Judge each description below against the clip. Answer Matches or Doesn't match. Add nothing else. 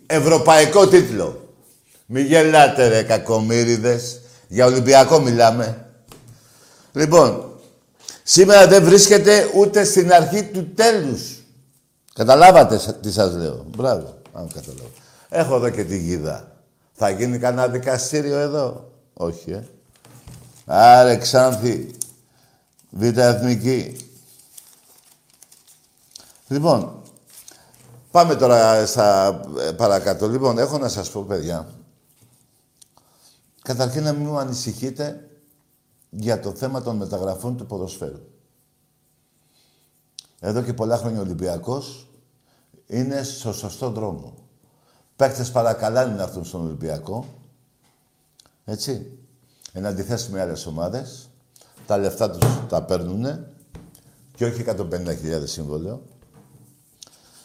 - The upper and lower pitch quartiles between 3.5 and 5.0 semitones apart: Matches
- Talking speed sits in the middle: Doesn't match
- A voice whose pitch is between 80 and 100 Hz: Doesn't match